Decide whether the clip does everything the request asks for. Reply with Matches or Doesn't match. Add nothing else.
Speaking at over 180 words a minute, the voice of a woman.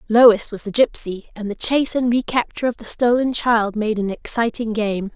Matches